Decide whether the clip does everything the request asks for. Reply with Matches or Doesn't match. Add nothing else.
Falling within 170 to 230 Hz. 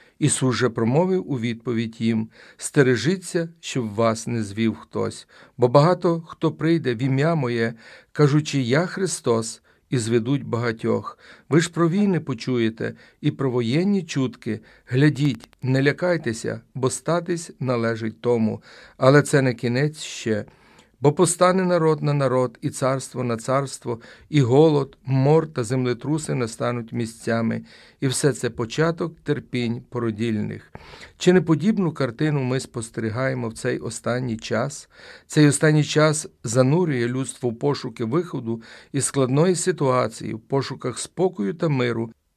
Doesn't match